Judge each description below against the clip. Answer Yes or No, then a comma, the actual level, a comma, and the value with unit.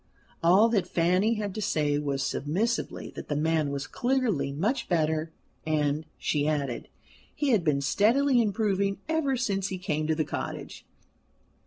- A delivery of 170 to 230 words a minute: No, average, 155 wpm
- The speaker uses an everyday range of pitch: No, wide, 6.3 semitones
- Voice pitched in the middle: Yes, medium, 175 Hz